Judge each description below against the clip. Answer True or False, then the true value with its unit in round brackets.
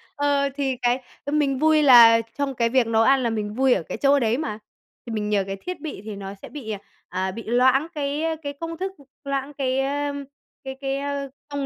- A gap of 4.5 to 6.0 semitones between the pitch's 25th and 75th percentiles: False (3.9 semitones)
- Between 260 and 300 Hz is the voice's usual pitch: True (270 Hz)